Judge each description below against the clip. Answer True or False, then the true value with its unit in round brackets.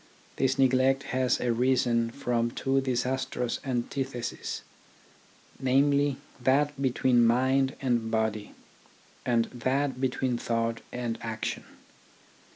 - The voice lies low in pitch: True (125 Hz)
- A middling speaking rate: False (95 wpm)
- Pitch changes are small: True (2.2 semitones)